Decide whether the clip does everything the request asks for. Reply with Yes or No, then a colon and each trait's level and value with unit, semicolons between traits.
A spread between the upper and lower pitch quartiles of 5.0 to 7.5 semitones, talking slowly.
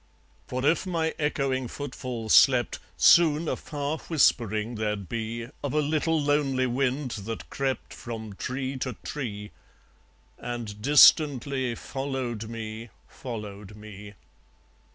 No: average, 4.3 semitones; slow, 115 wpm